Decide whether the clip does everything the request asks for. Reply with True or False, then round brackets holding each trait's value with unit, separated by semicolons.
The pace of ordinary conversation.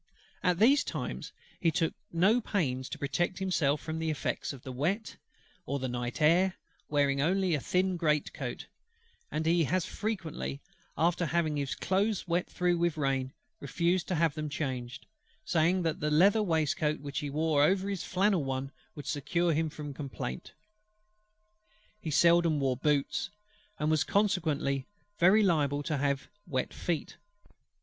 True (155 wpm)